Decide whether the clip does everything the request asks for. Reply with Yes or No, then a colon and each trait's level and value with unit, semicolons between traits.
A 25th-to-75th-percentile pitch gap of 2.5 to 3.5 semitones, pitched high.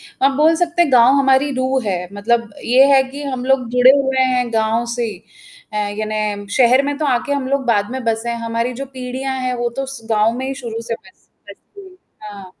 Yes: average, 2.9 semitones; very high, 250 Hz